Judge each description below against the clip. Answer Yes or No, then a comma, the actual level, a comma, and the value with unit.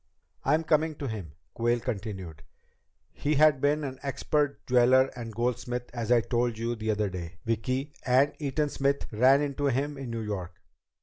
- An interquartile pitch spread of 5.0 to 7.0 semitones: No, average, 3.9 semitones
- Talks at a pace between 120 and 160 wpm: No, average, 170 wpm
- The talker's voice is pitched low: Yes, low, 125 Hz